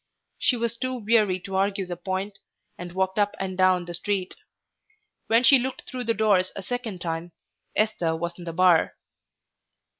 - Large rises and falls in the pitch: No, average, 3.7 semitones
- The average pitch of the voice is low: No, high, 190 Hz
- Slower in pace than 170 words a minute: No, average, 175 wpm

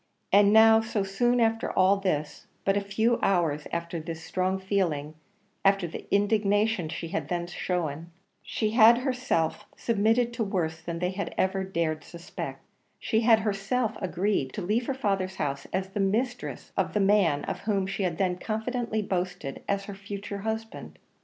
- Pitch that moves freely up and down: No, average, 3.9 semitones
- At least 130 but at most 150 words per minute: No, average, 170 wpm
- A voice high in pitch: Yes, high, 195 Hz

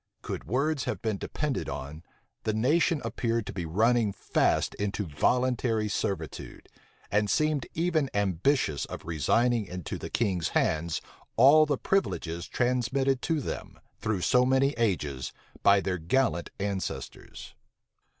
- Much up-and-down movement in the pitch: Yes, wide, 6.4 semitones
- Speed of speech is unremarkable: No, slow, 130 wpm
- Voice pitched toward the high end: No, low, 110 Hz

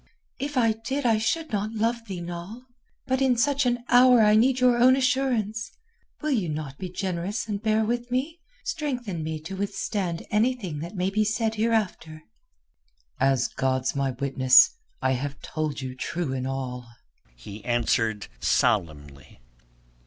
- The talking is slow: No, average, 155 wpm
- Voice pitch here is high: Yes, high, 205 Hz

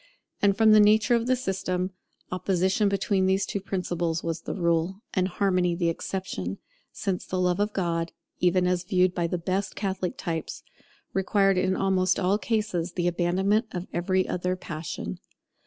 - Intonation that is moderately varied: No, narrow, 2.0 semitones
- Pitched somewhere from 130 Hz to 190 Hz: Yes, medium, 185 Hz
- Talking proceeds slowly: No, average, 165 wpm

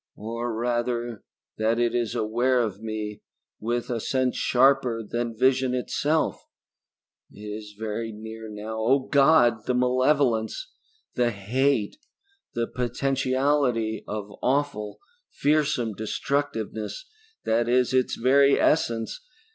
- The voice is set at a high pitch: No, low, 120 Hz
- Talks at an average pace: No, slow, 115 wpm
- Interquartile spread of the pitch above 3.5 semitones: No, average, 2.9 semitones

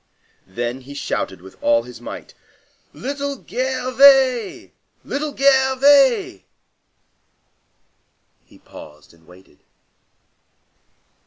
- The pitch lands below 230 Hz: No, very high, 250 Hz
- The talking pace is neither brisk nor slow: No, slow, 80 wpm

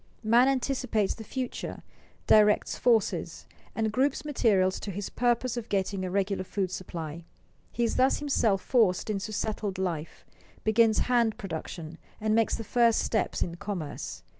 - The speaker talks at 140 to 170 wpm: Yes, average, 150 wpm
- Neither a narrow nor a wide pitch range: Yes, average, 4.0 semitones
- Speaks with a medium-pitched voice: No, high, 215 Hz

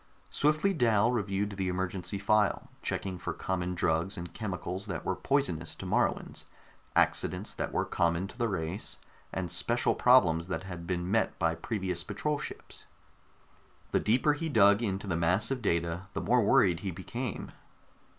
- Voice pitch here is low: Yes, very low, 95 Hz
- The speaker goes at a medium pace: Yes, average, 160 wpm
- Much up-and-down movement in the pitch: No, average, 3.9 semitones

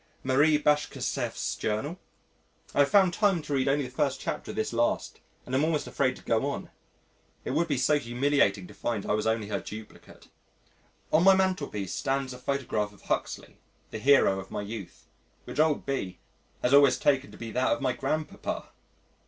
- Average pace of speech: Yes, average, 190 wpm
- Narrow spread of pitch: No, average, 4.8 semitones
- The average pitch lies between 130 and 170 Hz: Yes, low, 135 Hz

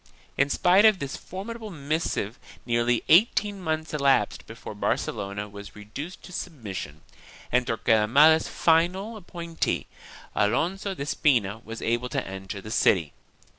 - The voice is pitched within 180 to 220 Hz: No, medium, 140 Hz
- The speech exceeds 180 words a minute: No, slow, 135 wpm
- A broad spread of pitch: Yes, wide, 8.1 semitones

